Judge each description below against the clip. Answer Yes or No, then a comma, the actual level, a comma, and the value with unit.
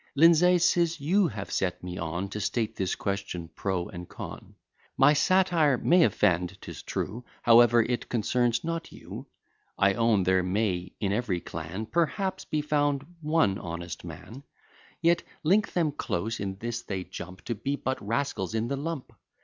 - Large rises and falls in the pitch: Yes, wide, 7.8 semitones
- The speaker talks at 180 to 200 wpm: No, average, 165 wpm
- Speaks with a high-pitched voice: No, low, 115 Hz